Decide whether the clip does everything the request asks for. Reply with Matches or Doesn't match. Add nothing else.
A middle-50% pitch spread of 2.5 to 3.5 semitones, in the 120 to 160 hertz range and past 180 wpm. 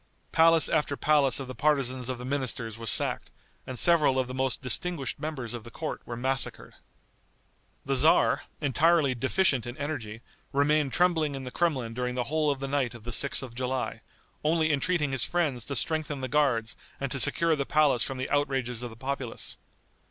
Matches